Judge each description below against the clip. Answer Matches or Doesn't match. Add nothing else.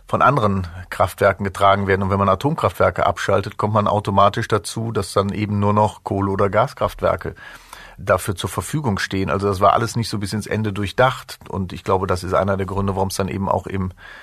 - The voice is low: Matches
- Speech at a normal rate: Doesn't match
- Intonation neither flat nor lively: Doesn't match